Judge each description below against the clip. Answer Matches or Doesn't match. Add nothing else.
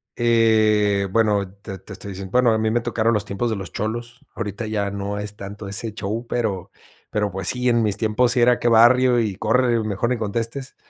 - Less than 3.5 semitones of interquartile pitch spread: Matches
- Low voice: Matches